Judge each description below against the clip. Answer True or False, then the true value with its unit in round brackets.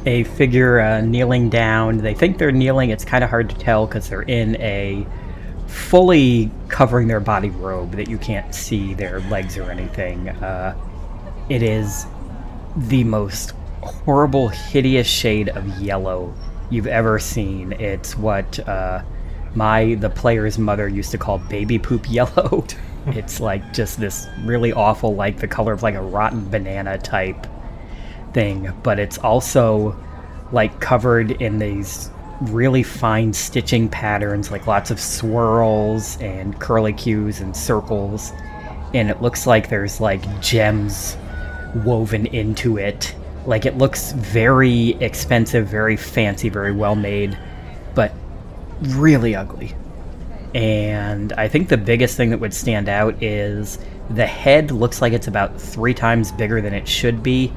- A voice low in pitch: True (110 Hz)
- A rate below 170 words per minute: True (145 wpm)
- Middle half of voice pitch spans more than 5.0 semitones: False (3.2 semitones)